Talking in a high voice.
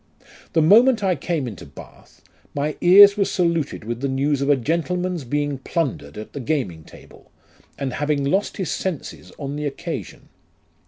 No: medium, 150 Hz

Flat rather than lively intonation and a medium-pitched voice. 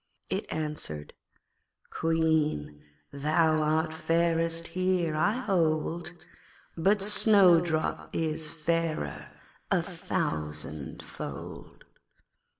Yes: narrow, 1.9 semitones; medium, 160 Hz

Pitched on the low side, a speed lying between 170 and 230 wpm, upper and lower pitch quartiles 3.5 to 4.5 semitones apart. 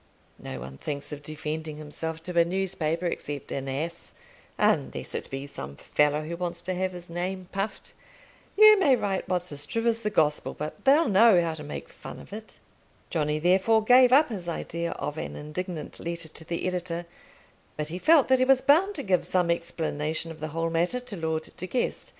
No: medium, 170 Hz; average, 200 wpm; average, 4.2 semitones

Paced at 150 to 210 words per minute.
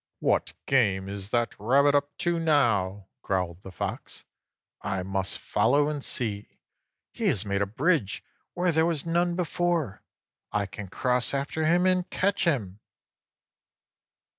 No: average, 140 wpm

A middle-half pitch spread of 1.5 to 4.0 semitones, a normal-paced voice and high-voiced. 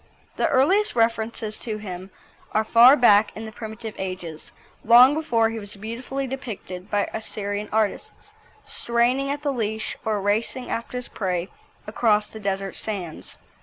Yes: average, 2.9 semitones; average, 150 wpm; high, 220 Hz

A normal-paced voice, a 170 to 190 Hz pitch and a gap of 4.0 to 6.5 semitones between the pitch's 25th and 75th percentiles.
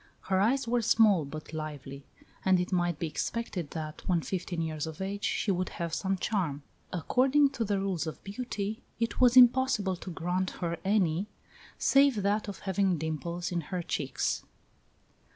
Yes: average, 170 wpm; medium, 185 Hz; average, 4.3 semitones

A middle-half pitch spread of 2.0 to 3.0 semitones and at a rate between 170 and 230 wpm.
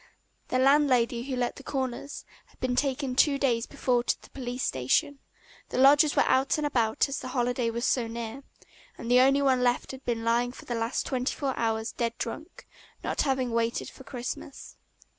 Yes: narrow, 2.4 semitones; average, 195 wpm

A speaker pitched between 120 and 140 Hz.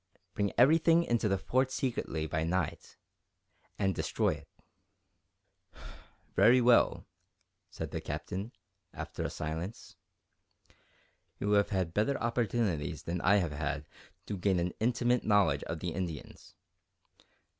No: low, 100 Hz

